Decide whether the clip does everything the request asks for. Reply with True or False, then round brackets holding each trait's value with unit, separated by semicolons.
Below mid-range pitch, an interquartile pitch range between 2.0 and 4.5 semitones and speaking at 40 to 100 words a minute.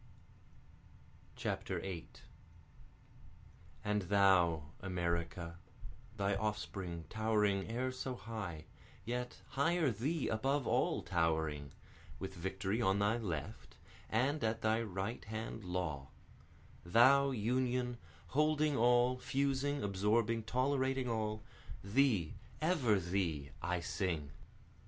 False (110 Hz; 5.6 semitones; 95 wpm)